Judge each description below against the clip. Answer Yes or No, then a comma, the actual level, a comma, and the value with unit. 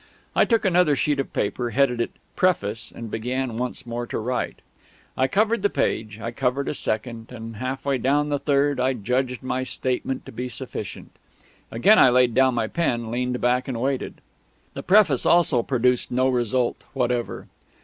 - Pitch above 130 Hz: No, low, 125 Hz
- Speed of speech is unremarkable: Yes, average, 180 wpm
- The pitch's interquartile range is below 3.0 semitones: Yes, narrow, 2.6 semitones